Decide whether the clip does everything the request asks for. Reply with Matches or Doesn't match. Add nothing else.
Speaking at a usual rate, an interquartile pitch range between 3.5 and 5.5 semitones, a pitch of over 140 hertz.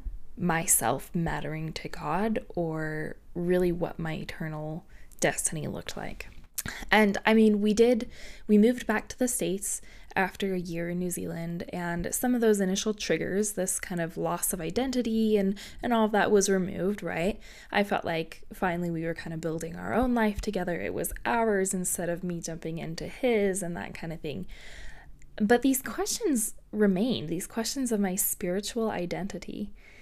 Matches